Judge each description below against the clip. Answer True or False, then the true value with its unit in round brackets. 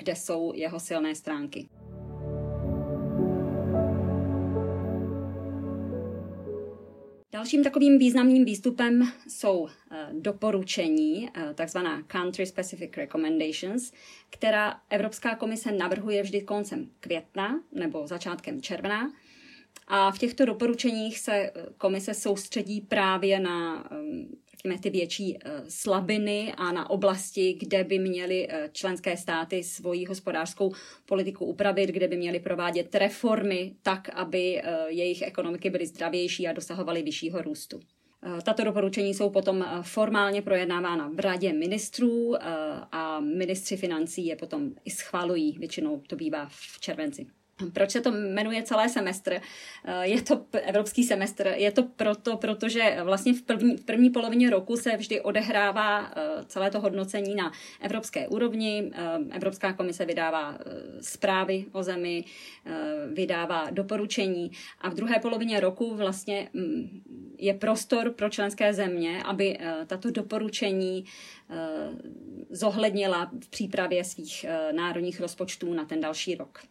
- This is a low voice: False (195 Hz)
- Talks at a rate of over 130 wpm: False (115 wpm)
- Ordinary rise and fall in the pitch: True (4.2 semitones)